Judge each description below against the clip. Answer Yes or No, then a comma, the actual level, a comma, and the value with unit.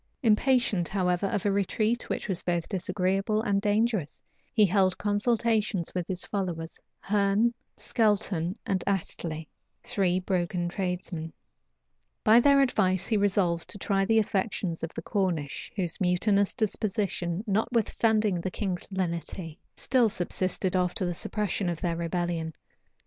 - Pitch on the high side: Yes, high, 195 Hz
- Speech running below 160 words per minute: Yes, slow, 135 wpm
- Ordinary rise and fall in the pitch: Yes, average, 3.2 semitones